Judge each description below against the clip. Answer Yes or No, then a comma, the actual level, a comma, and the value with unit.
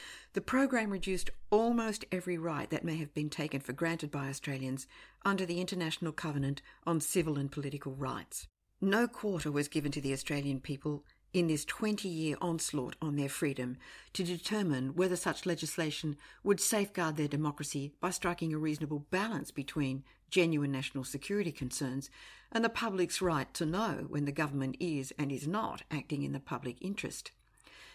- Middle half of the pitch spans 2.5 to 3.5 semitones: No, average, 4.4 semitones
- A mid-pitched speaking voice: Yes, medium, 155 Hz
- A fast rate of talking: No, average, 165 wpm